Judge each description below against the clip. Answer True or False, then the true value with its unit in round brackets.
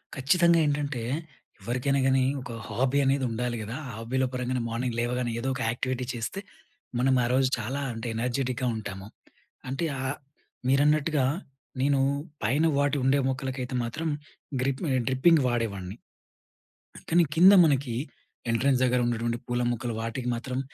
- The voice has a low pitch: True (130 Hz)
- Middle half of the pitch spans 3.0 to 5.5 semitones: False (2.6 semitones)